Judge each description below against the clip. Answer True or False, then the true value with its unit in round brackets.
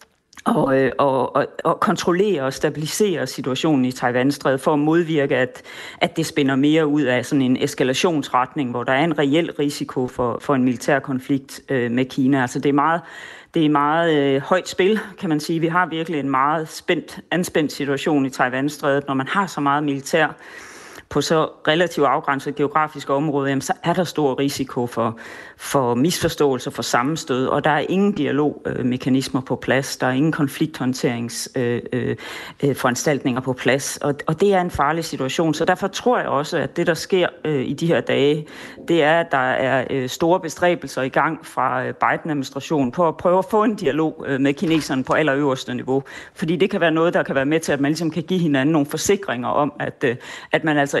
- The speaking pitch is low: False (145 Hz)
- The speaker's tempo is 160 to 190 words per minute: True (185 wpm)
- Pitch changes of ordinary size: True (3.5 semitones)